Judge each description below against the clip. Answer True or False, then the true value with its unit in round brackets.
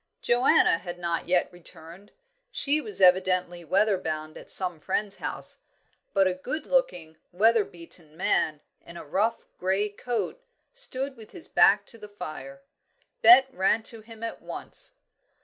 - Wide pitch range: False (4.9 semitones)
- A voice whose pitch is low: False (195 Hz)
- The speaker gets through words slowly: False (150 wpm)